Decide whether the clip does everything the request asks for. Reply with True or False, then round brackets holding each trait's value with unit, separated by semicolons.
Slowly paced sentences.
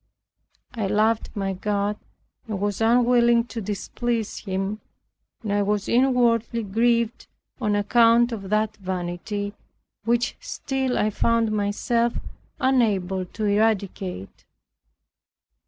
True (105 wpm)